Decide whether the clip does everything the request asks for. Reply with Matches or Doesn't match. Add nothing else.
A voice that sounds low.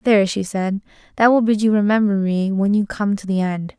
Doesn't match